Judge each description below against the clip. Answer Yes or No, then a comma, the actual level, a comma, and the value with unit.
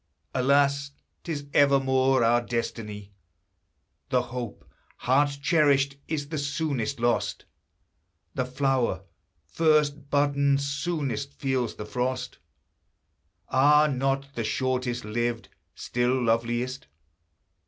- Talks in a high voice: No, low, 130 Hz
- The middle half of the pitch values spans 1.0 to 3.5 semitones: Yes, average, 2.8 semitones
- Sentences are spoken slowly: Yes, slow, 95 wpm